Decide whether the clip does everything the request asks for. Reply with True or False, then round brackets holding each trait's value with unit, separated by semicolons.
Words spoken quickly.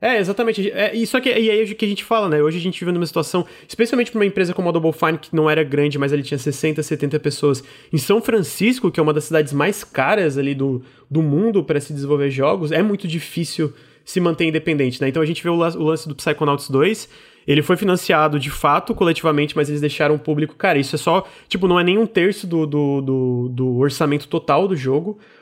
True (245 wpm)